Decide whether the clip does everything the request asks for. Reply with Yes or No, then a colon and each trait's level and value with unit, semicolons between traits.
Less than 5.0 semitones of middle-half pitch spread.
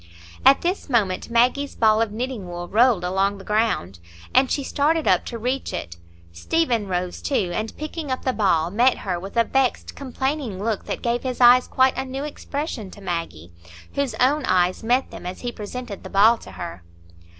No: wide, 5.6 semitones